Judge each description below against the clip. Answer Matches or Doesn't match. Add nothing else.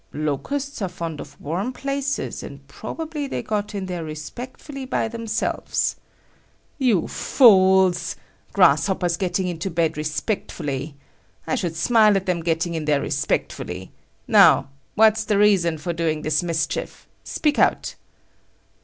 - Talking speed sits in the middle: Doesn't match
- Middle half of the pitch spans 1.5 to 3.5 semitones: Doesn't match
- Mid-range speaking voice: Matches